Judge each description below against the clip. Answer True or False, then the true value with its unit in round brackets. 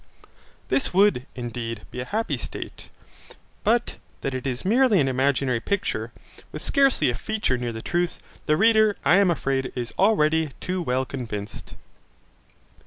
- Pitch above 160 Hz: False (150 Hz)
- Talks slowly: False (150 wpm)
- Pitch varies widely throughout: True (8.4 semitones)